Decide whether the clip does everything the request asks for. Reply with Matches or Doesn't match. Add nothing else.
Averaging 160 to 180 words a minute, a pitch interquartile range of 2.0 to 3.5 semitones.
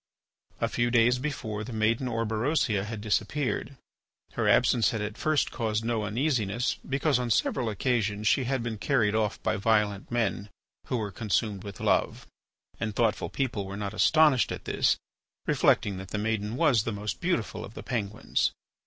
Matches